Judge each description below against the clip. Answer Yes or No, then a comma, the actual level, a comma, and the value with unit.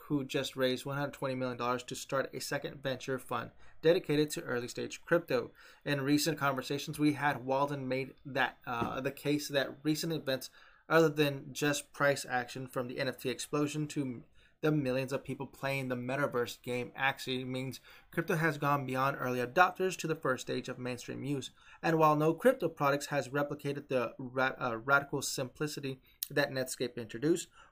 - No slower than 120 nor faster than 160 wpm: No, average, 170 wpm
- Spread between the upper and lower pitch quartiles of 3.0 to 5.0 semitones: No, narrow, 2.4 semitones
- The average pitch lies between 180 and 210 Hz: No, medium, 140 Hz